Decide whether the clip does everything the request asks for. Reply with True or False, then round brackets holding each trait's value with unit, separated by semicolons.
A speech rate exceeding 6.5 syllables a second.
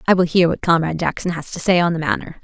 True (7.1 syllables/s)